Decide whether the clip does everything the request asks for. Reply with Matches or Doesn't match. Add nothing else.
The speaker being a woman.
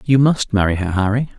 Doesn't match